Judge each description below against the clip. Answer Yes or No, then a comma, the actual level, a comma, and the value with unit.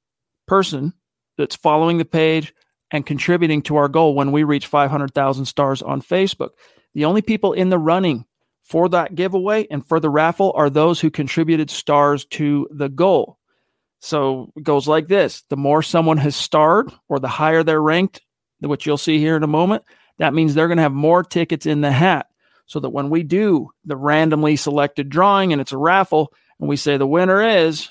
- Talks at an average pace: Yes, average, 195 wpm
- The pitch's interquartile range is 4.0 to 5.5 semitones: No, average, 2.7 semitones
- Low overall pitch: No, medium, 155 Hz